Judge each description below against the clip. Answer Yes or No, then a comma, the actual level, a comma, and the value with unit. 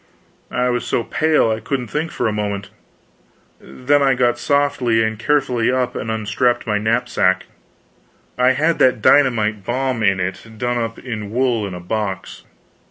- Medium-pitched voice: No, low, 120 Hz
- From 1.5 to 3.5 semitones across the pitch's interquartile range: Yes, average, 3.2 semitones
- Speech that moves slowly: No, average, 165 wpm